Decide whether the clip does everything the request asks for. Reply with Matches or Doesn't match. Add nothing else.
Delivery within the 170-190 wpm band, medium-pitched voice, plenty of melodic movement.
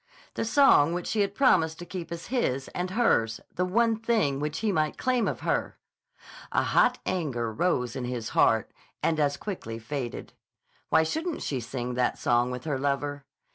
Matches